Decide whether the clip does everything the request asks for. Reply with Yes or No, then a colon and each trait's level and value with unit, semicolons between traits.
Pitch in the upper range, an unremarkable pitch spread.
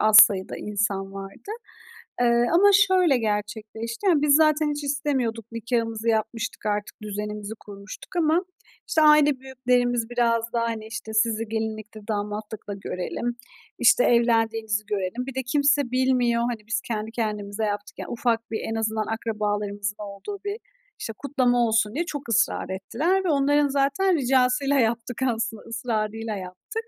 Yes: high, 230 Hz; average, 3.7 semitones